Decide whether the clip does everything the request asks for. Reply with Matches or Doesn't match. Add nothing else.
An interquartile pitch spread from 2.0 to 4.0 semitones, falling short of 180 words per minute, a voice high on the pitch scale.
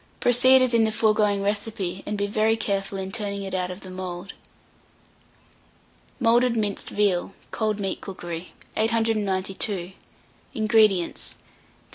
Matches